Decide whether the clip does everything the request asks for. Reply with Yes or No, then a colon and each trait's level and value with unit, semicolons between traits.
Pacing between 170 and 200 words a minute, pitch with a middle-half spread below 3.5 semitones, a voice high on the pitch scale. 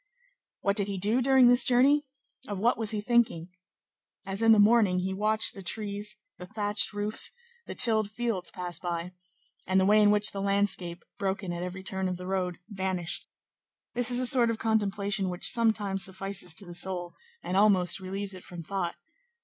Yes: average, 190 wpm; average, 2.8 semitones; high, 200 Hz